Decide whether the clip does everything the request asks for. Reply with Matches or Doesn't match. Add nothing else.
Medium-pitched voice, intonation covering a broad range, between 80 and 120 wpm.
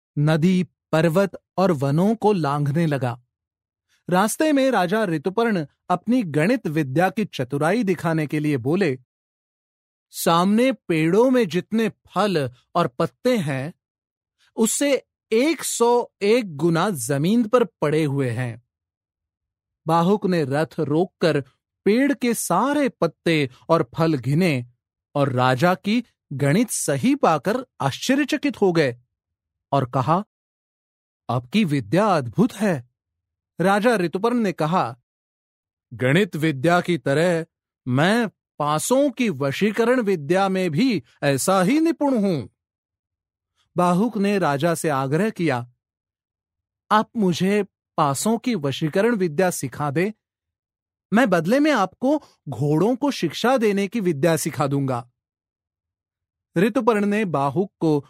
Matches